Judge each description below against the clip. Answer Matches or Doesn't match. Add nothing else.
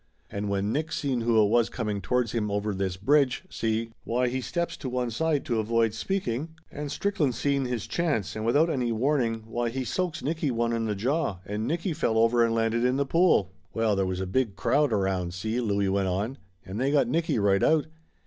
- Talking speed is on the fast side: Matches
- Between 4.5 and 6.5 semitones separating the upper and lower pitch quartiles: Matches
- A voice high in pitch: Doesn't match